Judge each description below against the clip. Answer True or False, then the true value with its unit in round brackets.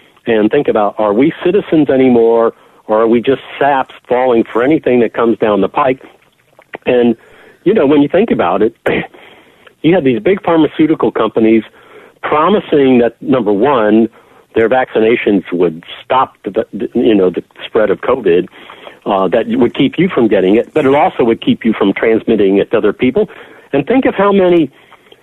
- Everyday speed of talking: True (175 wpm)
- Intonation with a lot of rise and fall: True (8.7 semitones)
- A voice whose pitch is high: False (135 Hz)